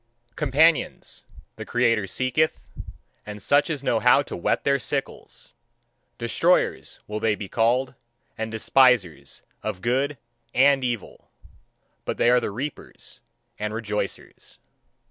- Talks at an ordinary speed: No, slow, 125 wpm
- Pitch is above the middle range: No, low, 120 Hz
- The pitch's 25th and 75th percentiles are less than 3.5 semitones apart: No, average, 4.2 semitones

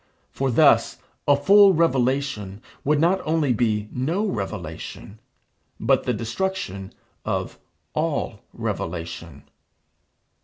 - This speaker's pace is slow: Yes, slow, 100 wpm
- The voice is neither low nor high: No, low, 130 Hz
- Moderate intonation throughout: No, wide, 7.8 semitones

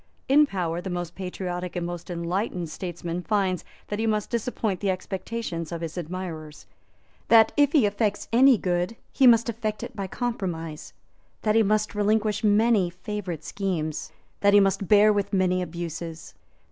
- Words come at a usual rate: Yes, average, 160 wpm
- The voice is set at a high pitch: Yes, high, 195 Hz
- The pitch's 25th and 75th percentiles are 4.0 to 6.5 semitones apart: No, average, 3.5 semitones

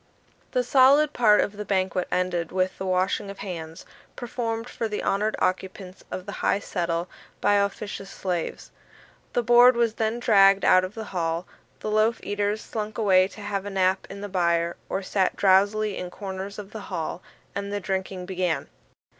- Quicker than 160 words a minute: Yes, average, 180 wpm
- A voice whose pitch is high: Yes, high, 195 Hz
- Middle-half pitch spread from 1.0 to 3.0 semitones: Yes, narrow, 2.5 semitones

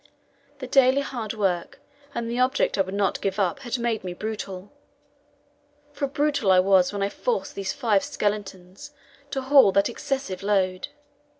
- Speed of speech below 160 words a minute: No, average, 165 wpm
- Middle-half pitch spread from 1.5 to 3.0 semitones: No, average, 5.2 semitones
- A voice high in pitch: Yes, high, 210 Hz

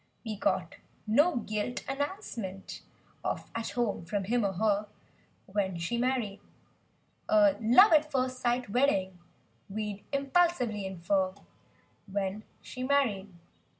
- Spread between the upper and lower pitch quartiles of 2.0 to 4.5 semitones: No, average, 5.0 semitones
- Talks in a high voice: Yes, high, 220 Hz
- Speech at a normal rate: No, slow, 115 wpm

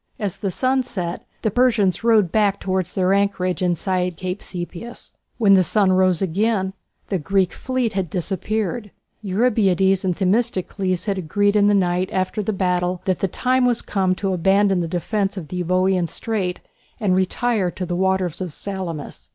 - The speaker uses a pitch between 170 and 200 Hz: Yes, high, 190 Hz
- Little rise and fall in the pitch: Yes, narrow, 2.2 semitones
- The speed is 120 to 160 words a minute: No, average, 170 wpm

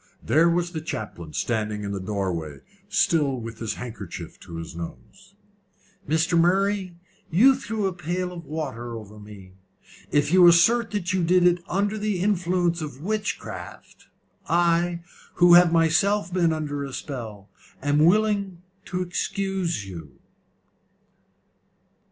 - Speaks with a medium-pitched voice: Yes, medium, 170 Hz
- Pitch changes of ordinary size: No, wide, 7.6 semitones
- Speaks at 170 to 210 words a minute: No, slow, 135 wpm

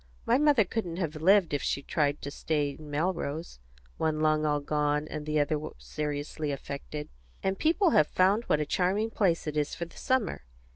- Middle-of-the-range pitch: Yes, medium, 155 Hz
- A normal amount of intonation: Yes, average, 4.1 semitones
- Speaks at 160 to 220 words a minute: Yes, average, 200 wpm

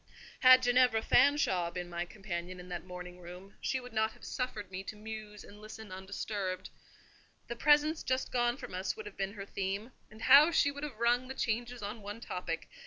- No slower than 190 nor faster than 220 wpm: Yes, average, 200 wpm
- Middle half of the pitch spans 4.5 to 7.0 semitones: Yes, average, 4.9 semitones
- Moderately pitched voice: No, high, 215 Hz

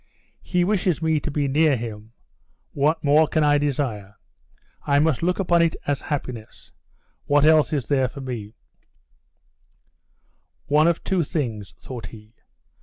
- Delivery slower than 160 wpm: Yes, average, 150 wpm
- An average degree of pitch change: Yes, average, 4.4 semitones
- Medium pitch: Yes, medium, 145 Hz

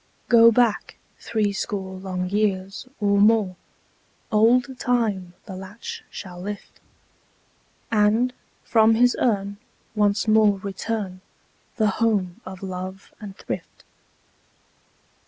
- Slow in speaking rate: Yes, slow, 100 wpm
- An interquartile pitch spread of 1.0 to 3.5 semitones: Yes, average, 2.8 semitones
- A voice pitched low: No, high, 205 Hz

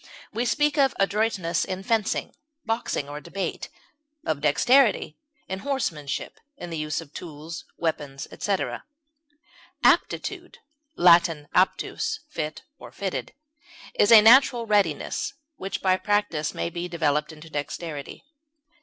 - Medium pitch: Yes, medium, 175 Hz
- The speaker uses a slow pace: Yes, slow, 120 wpm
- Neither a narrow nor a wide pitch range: No, wide, 5.7 semitones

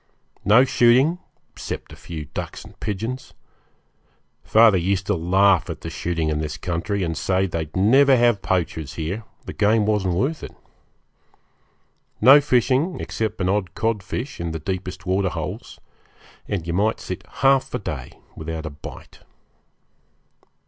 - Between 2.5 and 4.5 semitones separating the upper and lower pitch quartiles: No, average, 5.1 semitones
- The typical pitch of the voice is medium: No, very low, 95 Hz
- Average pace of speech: Yes, average, 145 wpm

